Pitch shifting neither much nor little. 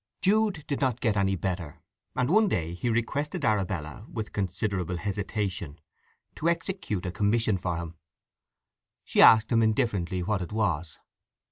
Yes: average, 5.0 semitones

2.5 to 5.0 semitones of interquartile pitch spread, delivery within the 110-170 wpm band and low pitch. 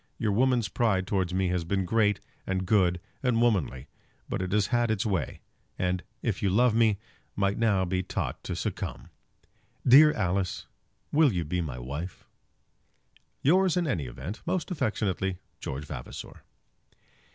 Yes: average, 4.3 semitones; average, 150 wpm; low, 100 Hz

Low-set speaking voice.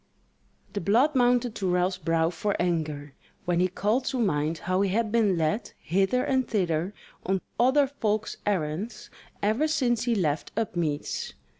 No: high, 200 Hz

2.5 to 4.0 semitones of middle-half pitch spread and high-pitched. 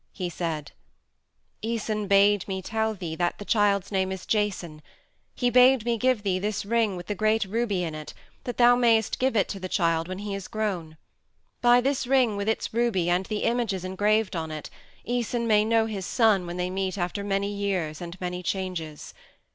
Yes: average, 3.5 semitones; high, 200 Hz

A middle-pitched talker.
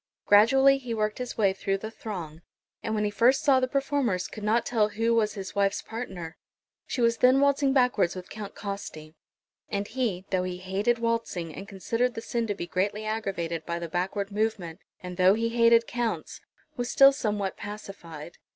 No: high, 210 Hz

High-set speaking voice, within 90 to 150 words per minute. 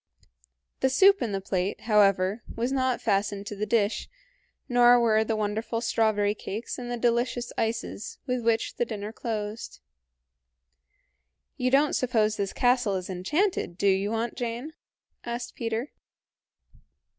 Yes: high, 225 Hz; average, 140 wpm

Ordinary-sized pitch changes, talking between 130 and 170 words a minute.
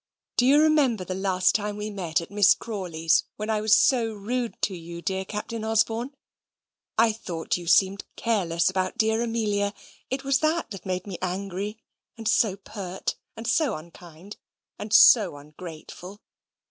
Yes: average, 3.5 semitones; average, 160 wpm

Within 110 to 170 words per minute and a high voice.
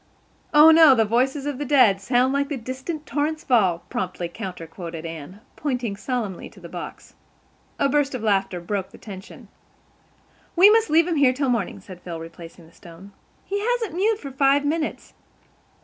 No: average, 180 wpm; very high, 255 Hz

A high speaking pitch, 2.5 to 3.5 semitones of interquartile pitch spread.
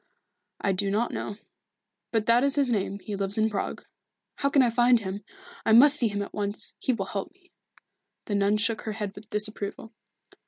Yes: high, 215 Hz; average, 2.9 semitones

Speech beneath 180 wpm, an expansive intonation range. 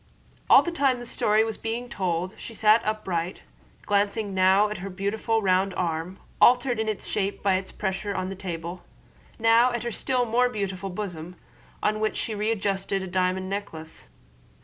No: average, 170 wpm; average, 3.1 semitones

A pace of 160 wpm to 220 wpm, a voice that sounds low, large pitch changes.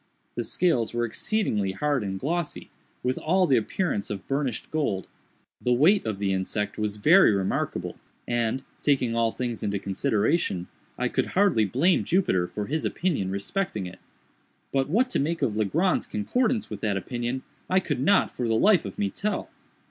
Yes: average, 170 wpm; low, 120 Hz; wide, 8.2 semitones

